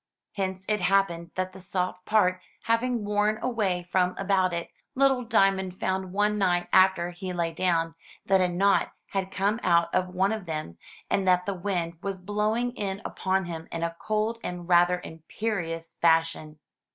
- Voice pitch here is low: No, medium, 185 Hz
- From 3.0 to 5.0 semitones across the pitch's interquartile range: No, narrow, 2.6 semitones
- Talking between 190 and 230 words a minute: No, average, 170 wpm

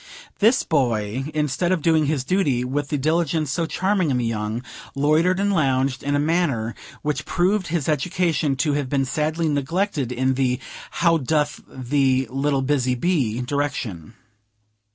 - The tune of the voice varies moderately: Yes, average, 4.1 semitones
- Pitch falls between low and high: Yes, medium, 145 Hz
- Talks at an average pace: Yes, average, 155 wpm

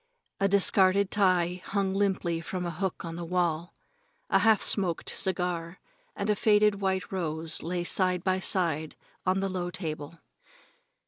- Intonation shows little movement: Yes, narrow, 2.3 semitones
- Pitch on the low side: No, medium, 185 Hz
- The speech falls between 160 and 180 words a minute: No, average, 150 wpm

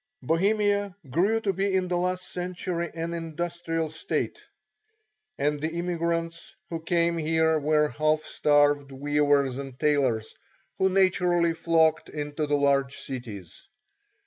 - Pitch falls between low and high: Yes, medium, 165 Hz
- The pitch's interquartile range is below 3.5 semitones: Yes, average, 3.1 semitones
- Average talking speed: No, slow, 125 wpm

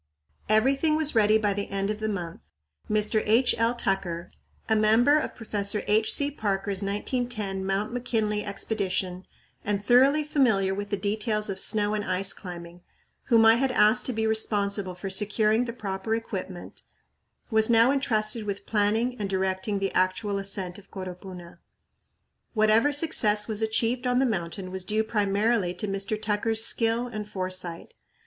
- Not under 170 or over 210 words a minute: No, average, 160 wpm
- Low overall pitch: No, high, 210 Hz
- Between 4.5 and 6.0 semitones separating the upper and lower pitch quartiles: No, narrow, 2.5 semitones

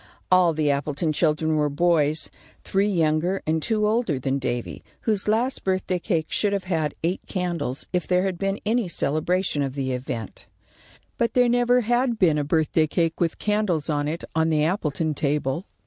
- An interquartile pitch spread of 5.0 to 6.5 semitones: No, average, 4.6 semitones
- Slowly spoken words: No, average, 180 wpm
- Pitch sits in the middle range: Yes, medium, 165 Hz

